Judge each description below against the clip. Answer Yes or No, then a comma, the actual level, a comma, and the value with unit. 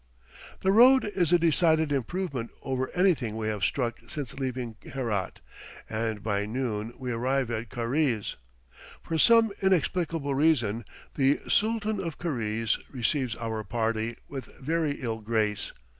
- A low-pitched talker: Yes, low, 130 Hz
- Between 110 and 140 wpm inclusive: Yes, slow, 135 wpm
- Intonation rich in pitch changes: Yes, wide, 6.3 semitones